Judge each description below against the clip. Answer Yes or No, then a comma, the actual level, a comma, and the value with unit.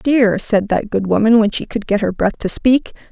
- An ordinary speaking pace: No, fast, 250 wpm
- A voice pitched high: Yes, high, 215 Hz